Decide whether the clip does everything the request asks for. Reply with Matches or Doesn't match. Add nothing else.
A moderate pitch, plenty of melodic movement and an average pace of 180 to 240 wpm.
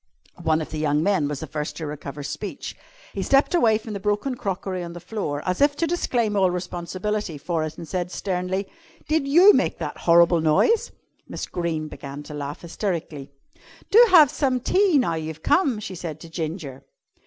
Matches